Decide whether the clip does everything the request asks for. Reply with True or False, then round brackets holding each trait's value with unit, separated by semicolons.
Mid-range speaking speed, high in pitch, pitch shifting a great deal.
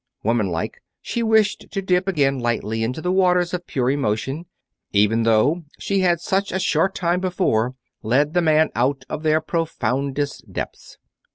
False (165 wpm; 155 Hz; 6.7 semitones)